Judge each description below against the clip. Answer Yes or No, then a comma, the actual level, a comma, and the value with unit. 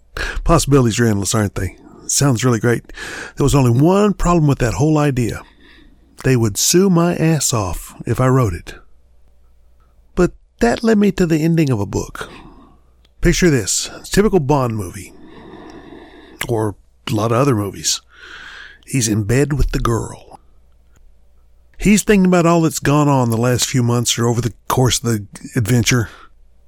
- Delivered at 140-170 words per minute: Yes, average, 165 wpm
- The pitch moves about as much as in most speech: No, wide, 7.9 semitones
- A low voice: Yes, low, 125 Hz